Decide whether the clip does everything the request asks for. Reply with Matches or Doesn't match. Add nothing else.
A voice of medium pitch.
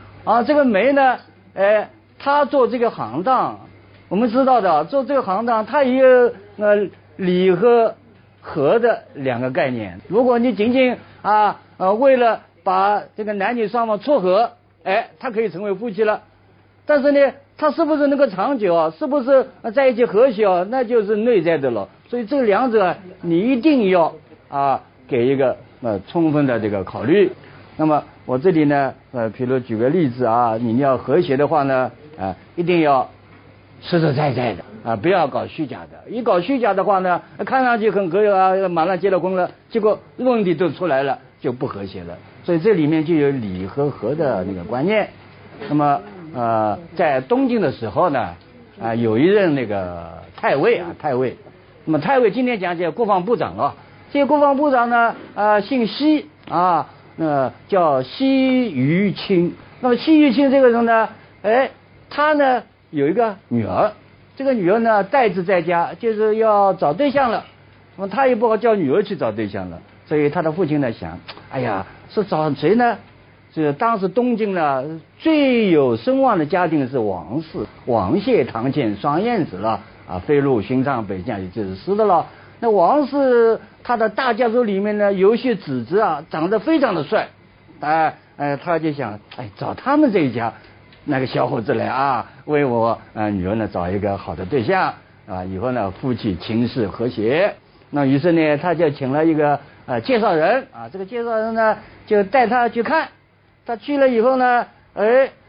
Matches